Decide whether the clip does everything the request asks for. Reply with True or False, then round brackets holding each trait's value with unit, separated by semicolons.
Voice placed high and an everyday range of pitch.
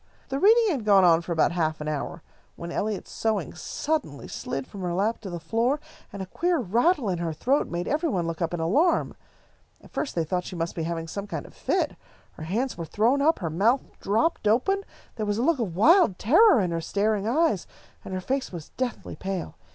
False (200 Hz; 7.6 semitones)